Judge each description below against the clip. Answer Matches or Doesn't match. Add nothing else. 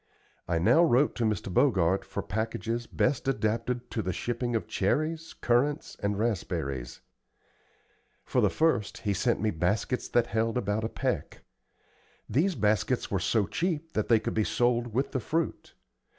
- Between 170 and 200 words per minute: Doesn't match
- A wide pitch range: Doesn't match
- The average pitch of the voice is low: Matches